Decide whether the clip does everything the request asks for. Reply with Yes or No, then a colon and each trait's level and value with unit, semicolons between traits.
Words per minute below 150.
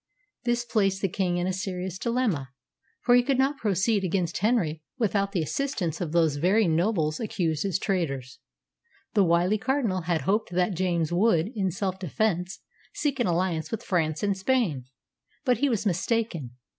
No: average, 170 wpm